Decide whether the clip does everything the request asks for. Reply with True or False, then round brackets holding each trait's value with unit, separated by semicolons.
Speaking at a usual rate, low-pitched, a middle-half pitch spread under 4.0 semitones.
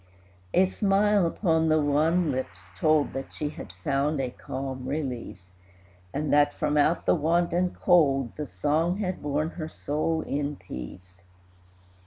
False (150 wpm; 150 Hz; 3.3 semitones)